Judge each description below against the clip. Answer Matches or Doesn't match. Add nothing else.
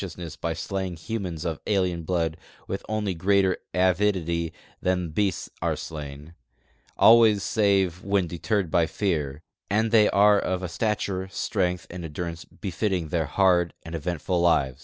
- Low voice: Matches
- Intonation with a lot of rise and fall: Doesn't match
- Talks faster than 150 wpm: Doesn't match